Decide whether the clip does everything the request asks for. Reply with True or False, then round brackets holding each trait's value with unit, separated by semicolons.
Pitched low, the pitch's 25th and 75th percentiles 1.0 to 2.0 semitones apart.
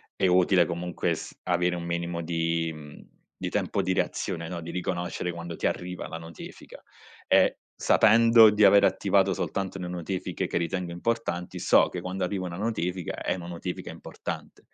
True (90 Hz; 1.6 semitones)